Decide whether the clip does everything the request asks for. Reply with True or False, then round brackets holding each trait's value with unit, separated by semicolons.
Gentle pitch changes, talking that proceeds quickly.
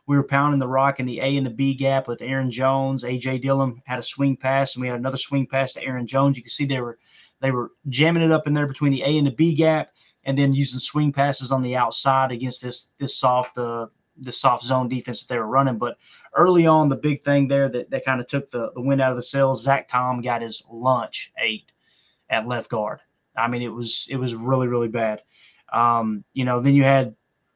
True (1.9 semitones; 245 wpm)